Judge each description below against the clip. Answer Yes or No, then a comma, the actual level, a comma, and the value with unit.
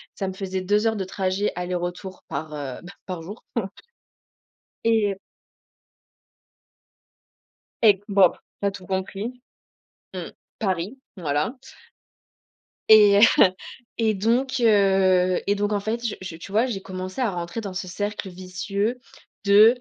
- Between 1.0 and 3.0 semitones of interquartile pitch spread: Yes, narrow, 2.5 semitones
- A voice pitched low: No, high, 195 Hz